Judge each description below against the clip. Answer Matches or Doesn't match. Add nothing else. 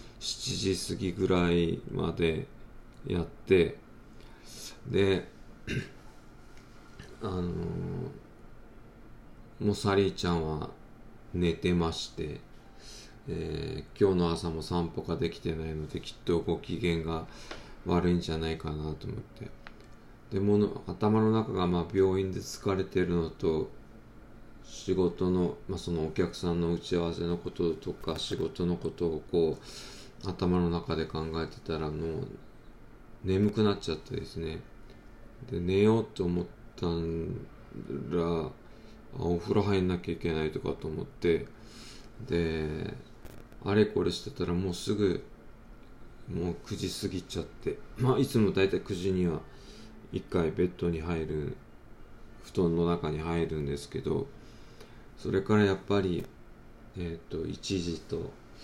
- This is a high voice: Doesn't match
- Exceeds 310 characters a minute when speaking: Doesn't match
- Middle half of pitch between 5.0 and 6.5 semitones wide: Doesn't match